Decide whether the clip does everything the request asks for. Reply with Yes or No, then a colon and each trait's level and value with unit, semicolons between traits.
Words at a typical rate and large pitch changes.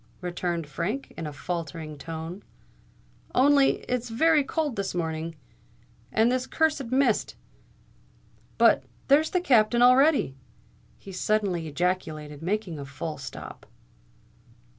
No: slow, 105 wpm; wide, 8.0 semitones